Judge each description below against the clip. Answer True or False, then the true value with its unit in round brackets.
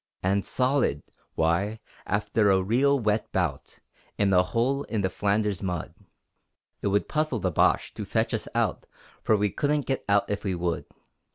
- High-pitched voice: False (105 Hz)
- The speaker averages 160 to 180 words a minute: True (170 wpm)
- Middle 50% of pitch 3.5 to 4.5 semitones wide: True (3.8 semitones)